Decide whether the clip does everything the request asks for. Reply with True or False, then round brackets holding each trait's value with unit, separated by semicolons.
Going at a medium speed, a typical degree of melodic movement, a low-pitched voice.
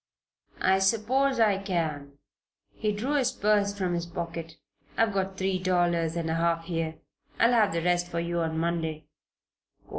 False (160 wpm; 3.4 semitones; 175 Hz)